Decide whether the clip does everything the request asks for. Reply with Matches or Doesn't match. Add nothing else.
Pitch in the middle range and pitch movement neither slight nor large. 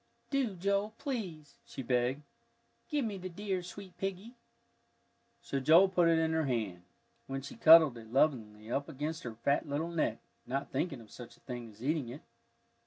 Doesn't match